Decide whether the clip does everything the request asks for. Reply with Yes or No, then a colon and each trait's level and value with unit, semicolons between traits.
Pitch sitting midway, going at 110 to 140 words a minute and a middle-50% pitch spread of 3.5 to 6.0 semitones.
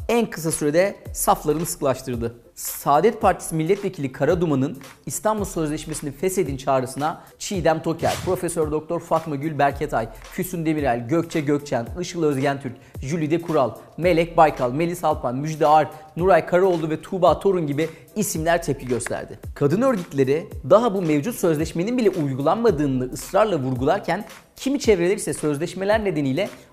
Yes: medium, 160 Hz; average, 130 wpm; average, 3.9 semitones